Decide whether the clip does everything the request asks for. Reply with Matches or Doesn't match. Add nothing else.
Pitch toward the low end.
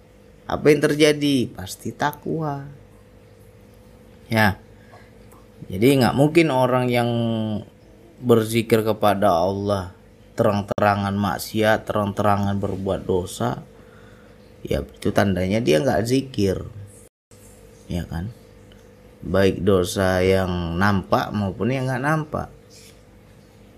Matches